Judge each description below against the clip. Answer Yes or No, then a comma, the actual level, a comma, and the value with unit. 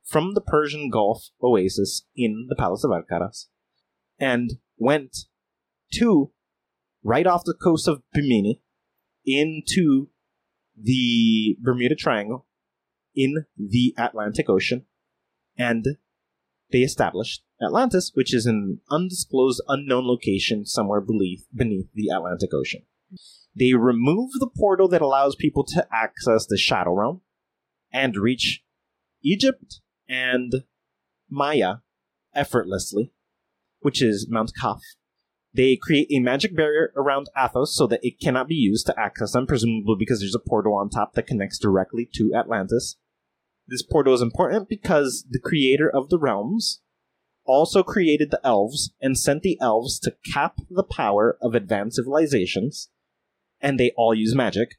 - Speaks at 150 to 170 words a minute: No, slow, 135 wpm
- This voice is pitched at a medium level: No, low, 130 Hz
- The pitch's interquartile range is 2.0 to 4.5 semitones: No, average, 5.2 semitones